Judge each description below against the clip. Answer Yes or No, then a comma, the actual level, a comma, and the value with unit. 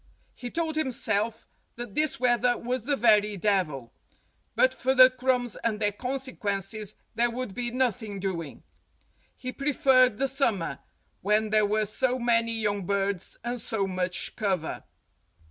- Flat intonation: No, average, 3.9 semitones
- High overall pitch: Yes, high, 230 Hz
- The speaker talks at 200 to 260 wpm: No, average, 145 wpm